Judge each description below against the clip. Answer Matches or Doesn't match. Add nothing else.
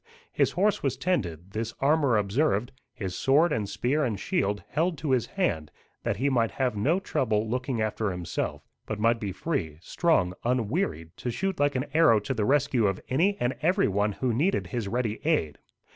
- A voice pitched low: Matches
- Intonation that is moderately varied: Doesn't match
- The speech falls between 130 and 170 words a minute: Doesn't match